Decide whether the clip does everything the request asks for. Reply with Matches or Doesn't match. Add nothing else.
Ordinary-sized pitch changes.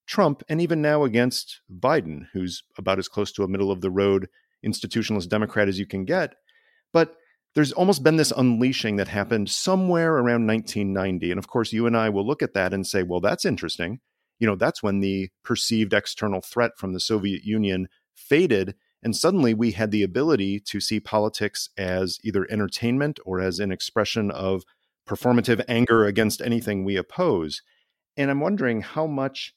Matches